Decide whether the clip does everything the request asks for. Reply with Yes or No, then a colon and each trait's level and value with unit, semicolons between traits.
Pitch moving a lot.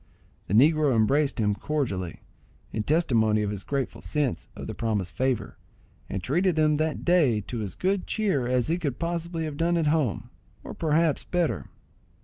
Yes: wide, 6.6 semitones